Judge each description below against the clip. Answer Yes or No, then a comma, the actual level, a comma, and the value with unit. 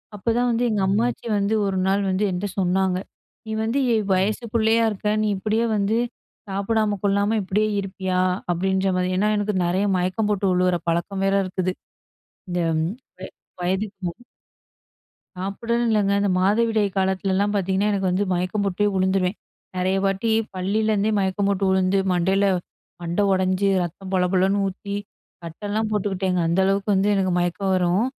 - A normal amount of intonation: No, narrow, 1.9 semitones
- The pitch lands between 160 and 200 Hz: Yes, high, 195 Hz